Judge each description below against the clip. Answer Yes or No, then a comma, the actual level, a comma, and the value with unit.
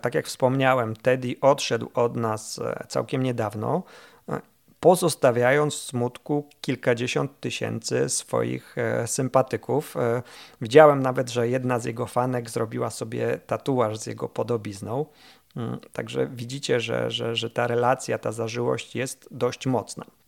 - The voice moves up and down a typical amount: No, narrow, 2.3 semitones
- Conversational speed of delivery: Yes, average, 120 wpm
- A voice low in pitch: Yes, low, 125 Hz